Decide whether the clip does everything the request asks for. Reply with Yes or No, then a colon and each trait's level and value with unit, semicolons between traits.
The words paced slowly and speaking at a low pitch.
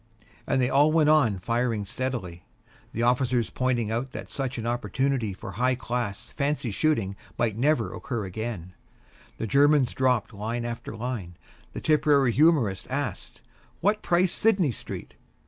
Yes: slow, 125 wpm; low, 125 Hz